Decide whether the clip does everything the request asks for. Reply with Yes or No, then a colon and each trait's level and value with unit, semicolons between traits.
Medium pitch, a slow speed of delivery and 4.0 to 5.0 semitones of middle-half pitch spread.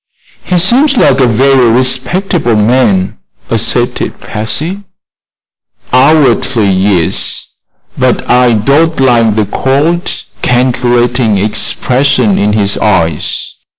No: low, 125 Hz; slow, 95 wpm; average, 4.6 semitones